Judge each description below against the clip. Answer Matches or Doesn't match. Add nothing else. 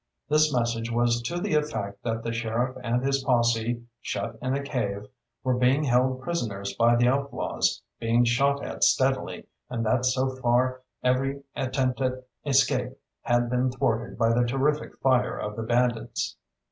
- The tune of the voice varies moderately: Doesn't match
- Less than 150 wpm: Doesn't match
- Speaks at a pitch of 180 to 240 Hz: Doesn't match